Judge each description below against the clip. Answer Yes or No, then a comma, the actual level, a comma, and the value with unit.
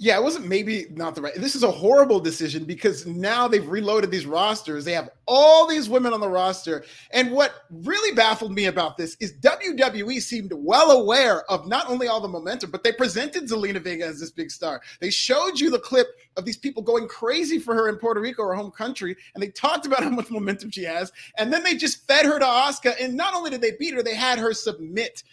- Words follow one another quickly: Yes, fast, 235 wpm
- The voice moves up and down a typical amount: No, wide, 5.9 semitones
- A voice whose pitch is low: No, high, 225 Hz